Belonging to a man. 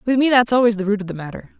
No: female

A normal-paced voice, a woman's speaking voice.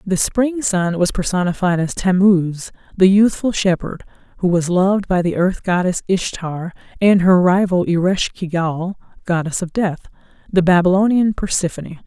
Yes: average, 150 wpm; female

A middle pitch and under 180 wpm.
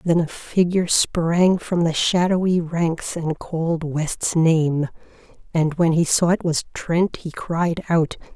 Yes: medium, 165 Hz; average, 160 wpm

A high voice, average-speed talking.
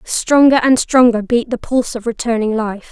Yes: high, 235 Hz; average, 185 wpm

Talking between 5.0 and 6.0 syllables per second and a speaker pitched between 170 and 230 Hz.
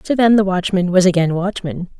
Yes: 5.5 syllables/s; medium, 185 Hz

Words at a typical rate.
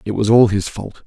No: fast, 280 wpm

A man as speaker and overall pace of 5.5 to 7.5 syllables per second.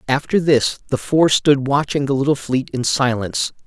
No: male; 4.9 syllables/s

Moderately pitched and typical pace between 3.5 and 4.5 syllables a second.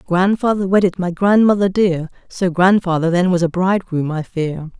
No: medium, 180 Hz; 5.0 syllables/s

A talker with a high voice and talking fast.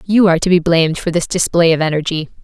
No: medium, 170 Hz; fast, 245 wpm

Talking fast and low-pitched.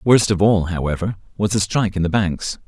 Yes: fast, 225 wpm; very low, 95 Hz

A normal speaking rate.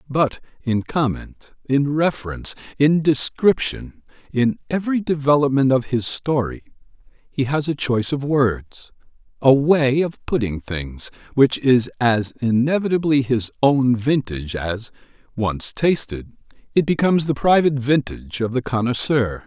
No: slow, 130 wpm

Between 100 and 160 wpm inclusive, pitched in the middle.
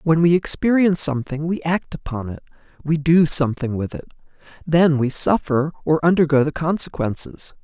Yes: average, 155 wpm; medium, 155 Hz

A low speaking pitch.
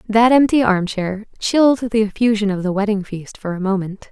No: high, 210 Hz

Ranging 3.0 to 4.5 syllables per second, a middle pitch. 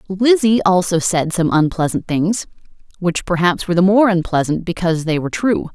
No: 5.5 syllables/s; medium, 180 Hz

